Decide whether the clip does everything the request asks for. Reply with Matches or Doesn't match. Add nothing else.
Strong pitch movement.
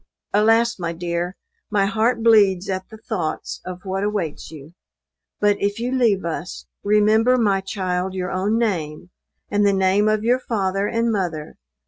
Doesn't match